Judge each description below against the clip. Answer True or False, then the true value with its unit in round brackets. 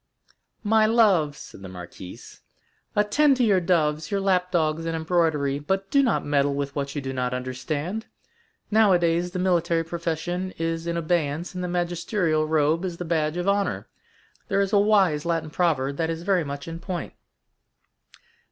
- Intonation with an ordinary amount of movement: True (3.6 semitones)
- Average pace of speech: True (170 wpm)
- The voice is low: False (170 Hz)